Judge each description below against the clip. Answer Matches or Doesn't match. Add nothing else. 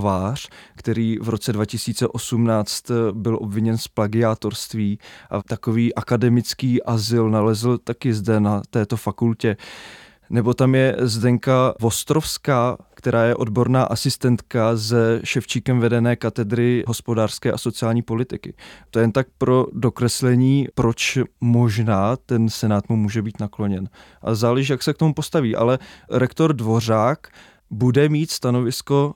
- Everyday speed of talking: Matches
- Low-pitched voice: Matches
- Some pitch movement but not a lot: Doesn't match